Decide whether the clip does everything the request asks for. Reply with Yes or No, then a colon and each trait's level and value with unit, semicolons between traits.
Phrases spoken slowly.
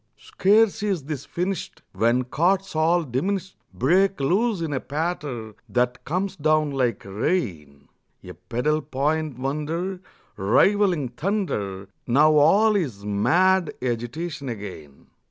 Yes: slow, 120 wpm